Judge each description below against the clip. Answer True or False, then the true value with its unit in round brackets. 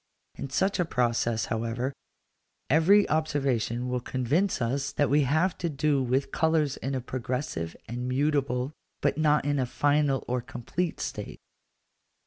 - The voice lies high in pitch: False (135 Hz)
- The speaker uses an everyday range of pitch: True (3.3 semitones)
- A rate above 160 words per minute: False (145 wpm)